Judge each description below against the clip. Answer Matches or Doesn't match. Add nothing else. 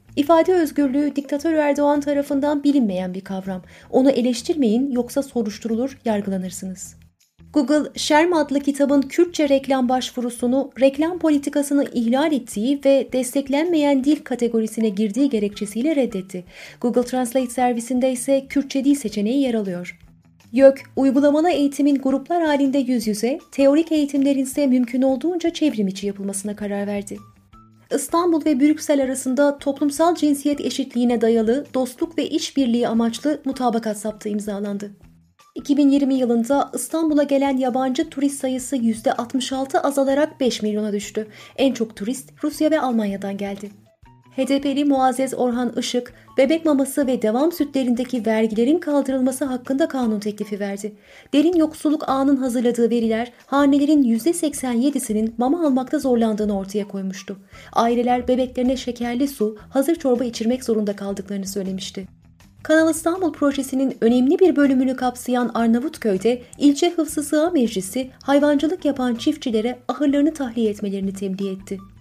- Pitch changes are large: Doesn't match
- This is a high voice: Matches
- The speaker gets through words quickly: Doesn't match